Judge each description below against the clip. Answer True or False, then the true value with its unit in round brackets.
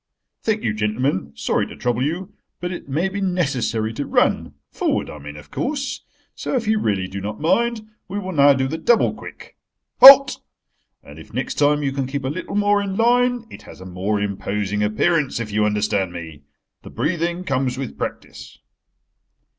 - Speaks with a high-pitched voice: False (140 Hz)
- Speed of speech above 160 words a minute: True (180 wpm)